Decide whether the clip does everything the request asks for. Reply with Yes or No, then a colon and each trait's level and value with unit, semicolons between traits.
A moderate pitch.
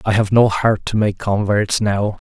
No: low, 105 Hz